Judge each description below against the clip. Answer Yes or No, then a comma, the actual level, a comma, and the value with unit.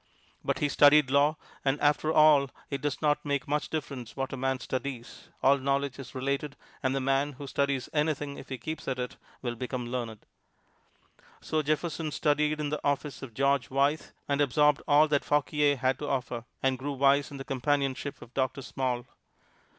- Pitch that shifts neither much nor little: No, narrow, 1.9 semitones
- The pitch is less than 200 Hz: Yes, medium, 140 Hz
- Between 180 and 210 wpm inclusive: Yes, average, 185 wpm